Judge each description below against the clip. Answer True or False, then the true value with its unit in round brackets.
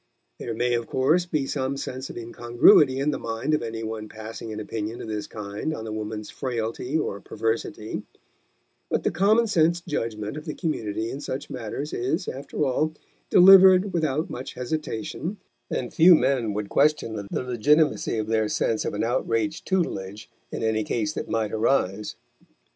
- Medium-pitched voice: False (120 Hz)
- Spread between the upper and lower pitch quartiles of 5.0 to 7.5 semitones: True (5.6 semitones)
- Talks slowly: False (170 wpm)